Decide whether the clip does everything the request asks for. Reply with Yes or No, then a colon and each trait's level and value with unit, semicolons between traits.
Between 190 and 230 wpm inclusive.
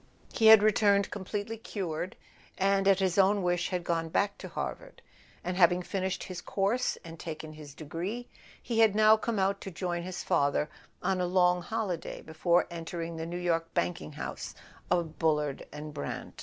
No: average, 175 wpm